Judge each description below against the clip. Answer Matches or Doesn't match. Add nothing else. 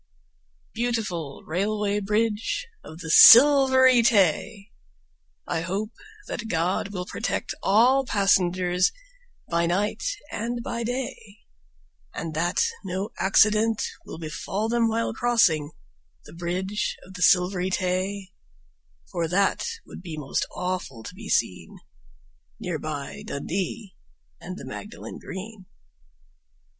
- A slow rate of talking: Matches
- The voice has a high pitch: Matches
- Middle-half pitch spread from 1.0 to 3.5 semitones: Doesn't match